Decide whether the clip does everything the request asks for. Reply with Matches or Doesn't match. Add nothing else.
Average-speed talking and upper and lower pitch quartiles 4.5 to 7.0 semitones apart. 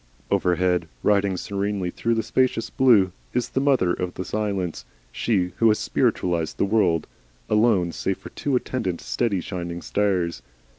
Doesn't match